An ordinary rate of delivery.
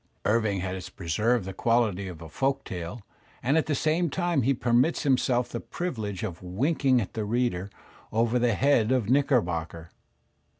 Yes: average, 165 wpm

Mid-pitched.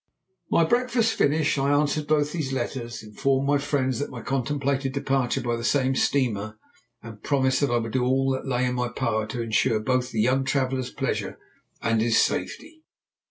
No: low, 130 Hz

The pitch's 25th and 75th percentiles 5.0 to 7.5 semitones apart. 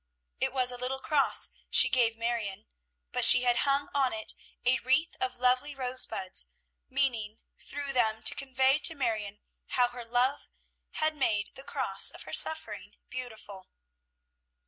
No: average, 2.9 semitones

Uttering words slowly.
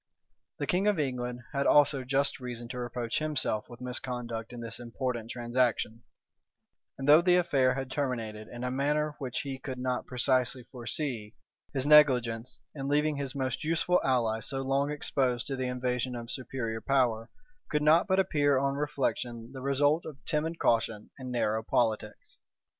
No: average, 165 wpm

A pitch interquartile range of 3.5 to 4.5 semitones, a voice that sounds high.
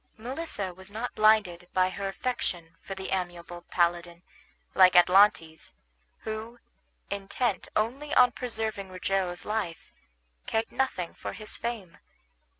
Yes: average, 3.9 semitones; high, 195 Hz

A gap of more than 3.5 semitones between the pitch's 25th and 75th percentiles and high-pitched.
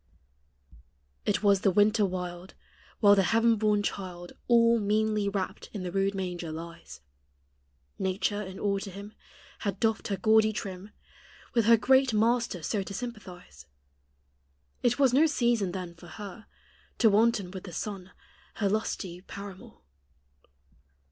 No: average, 3.0 semitones; high, 200 Hz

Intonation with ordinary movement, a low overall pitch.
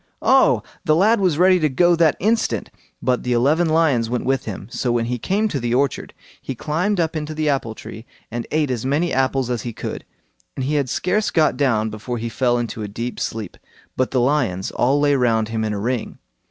Yes: average, 4.8 semitones; low, 130 Hz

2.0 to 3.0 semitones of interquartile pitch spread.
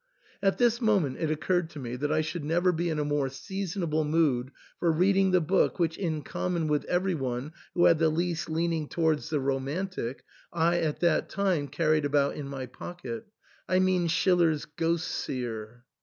No: average, 3.4 semitones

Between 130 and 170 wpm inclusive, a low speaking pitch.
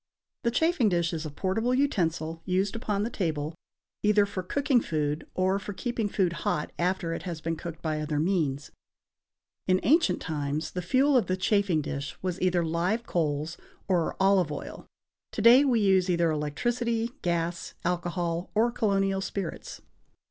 No: average, 165 wpm; medium, 185 Hz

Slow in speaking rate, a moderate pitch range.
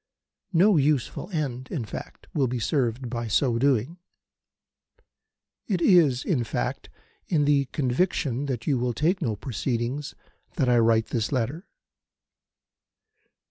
Yes: slow, 130 wpm; average, 4.1 semitones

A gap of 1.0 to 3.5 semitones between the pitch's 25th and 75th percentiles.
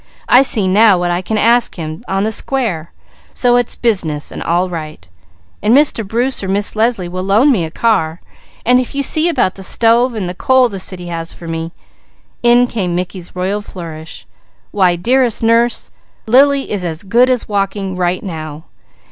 No: average, 5.3 semitones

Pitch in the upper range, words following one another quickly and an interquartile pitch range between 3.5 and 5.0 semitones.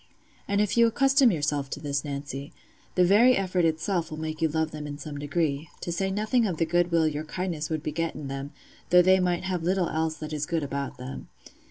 No: medium, 160 Hz; fast, 215 wpm; average, 3.8 semitones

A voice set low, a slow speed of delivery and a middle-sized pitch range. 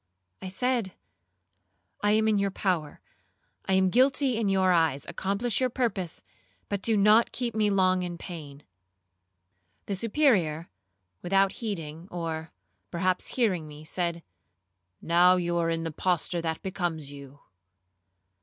No: medium, 185 Hz; slow, 130 wpm; average, 3.9 semitones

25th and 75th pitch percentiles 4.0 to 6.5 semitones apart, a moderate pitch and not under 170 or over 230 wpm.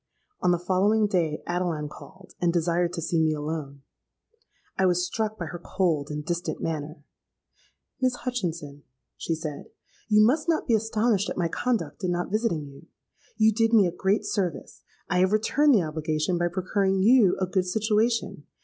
Yes: average, 4.7 semitones; medium, 180 Hz; average, 175 wpm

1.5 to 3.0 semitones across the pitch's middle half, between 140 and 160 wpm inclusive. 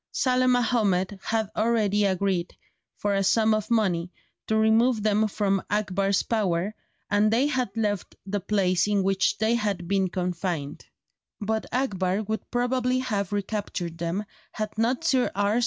Yes: average, 2.7 semitones; average, 150 wpm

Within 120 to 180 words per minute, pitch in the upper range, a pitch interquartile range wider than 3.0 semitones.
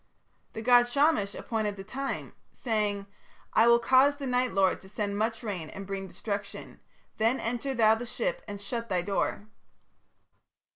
Yes: average, 160 wpm; high, 220 Hz; average, 3.6 semitones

